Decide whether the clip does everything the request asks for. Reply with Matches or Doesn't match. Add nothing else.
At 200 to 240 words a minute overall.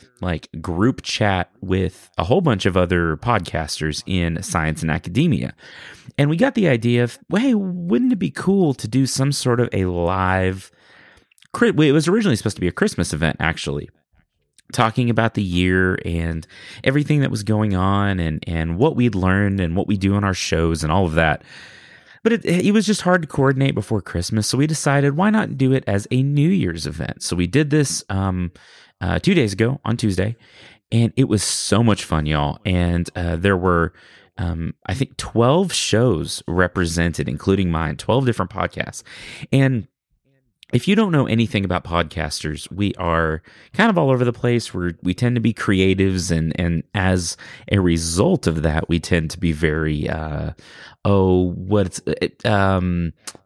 Doesn't match